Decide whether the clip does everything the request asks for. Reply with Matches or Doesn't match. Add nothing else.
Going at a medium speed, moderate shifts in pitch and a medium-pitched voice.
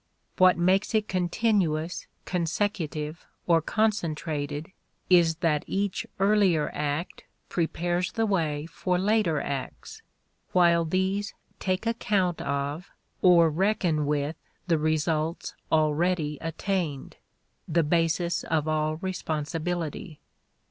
Doesn't match